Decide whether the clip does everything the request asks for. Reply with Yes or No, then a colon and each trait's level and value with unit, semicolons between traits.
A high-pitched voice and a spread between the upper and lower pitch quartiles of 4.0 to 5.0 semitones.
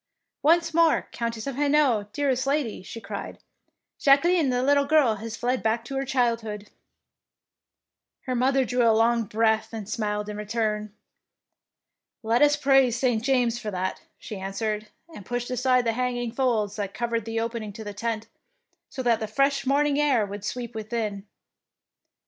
No: high, 235 Hz; average, 3.6 semitones